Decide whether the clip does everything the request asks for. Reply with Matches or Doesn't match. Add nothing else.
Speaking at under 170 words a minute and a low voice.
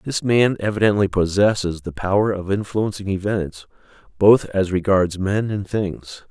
Matches